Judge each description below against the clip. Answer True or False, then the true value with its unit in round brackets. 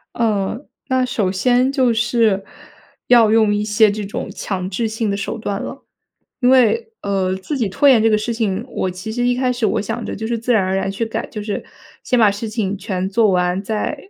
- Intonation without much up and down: False (3.3 semitones)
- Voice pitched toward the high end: True (220 Hz)